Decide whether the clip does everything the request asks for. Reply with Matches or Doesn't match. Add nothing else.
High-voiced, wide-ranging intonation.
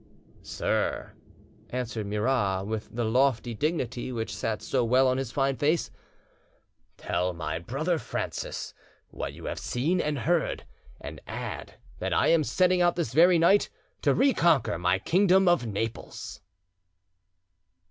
Doesn't match